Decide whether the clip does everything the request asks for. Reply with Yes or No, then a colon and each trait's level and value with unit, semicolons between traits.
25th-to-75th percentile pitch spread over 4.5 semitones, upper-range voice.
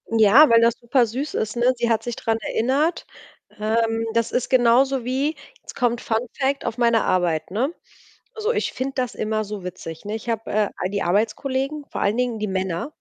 No: average, 3.3 semitones; high, 230 Hz